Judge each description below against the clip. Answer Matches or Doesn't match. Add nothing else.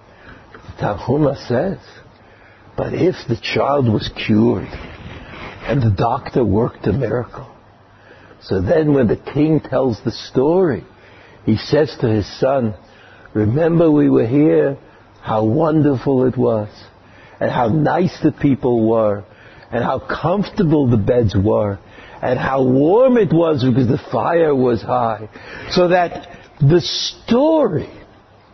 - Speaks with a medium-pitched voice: Doesn't match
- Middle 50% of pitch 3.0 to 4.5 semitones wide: Doesn't match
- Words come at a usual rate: Doesn't match